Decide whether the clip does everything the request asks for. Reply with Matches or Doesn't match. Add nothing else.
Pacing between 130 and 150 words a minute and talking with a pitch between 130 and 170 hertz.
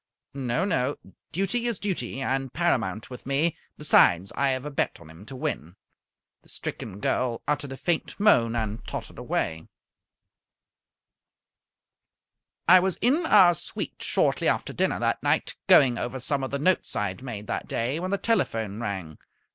Doesn't match